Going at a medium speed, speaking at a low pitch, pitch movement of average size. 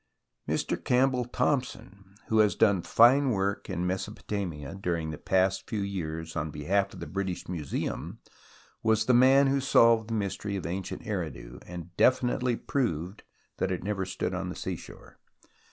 Yes: average, 155 wpm; low, 100 Hz; average, 4.6 semitones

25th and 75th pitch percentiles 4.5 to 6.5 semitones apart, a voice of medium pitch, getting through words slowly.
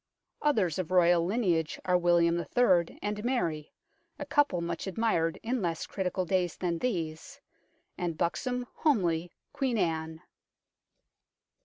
Yes: average, 5.0 semitones; medium, 180 Hz; slow, 125 wpm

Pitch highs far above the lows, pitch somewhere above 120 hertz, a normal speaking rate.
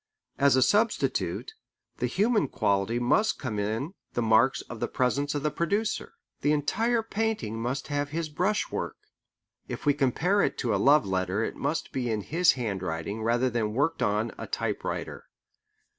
Yes: wide, 6.6 semitones; low, 135 Hz; average, 165 wpm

